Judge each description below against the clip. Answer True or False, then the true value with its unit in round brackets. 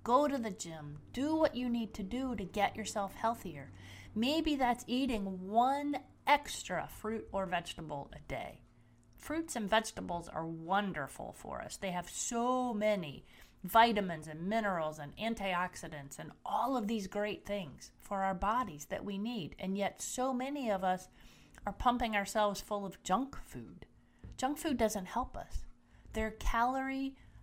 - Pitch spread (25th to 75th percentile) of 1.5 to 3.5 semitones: False (5.0 semitones)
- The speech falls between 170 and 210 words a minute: False (160 wpm)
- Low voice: False (210 Hz)